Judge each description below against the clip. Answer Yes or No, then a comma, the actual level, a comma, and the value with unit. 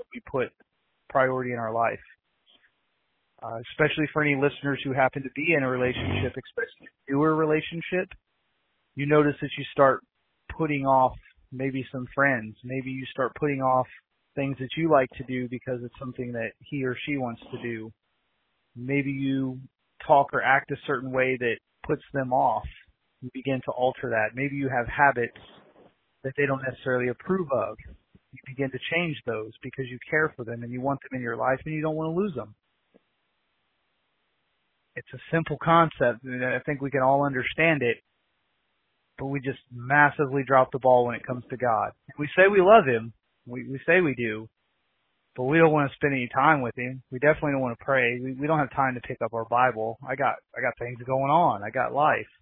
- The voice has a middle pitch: No, low, 130 Hz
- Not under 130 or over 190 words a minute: No, average, 200 wpm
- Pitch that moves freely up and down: No, narrow, 2.6 semitones